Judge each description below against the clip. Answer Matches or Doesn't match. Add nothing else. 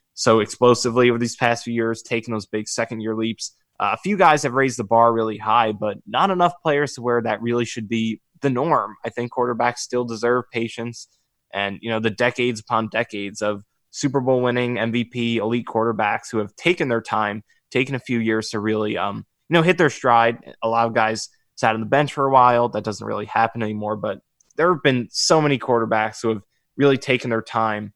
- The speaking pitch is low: Matches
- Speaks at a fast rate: Matches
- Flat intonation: Matches